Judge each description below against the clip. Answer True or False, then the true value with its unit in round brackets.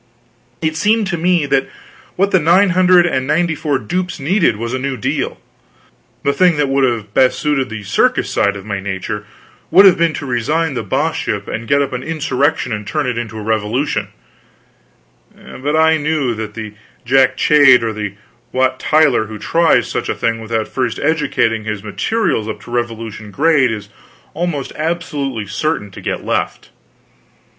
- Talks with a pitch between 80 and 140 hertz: True (135 Hz)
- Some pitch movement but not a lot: False (6.2 semitones)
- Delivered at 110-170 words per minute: False (180 wpm)